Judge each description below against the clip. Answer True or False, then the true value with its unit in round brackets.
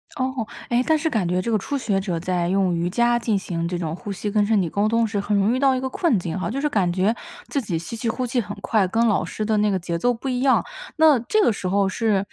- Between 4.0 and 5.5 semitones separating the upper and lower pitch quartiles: True (4.7 semitones)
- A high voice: True (210 Hz)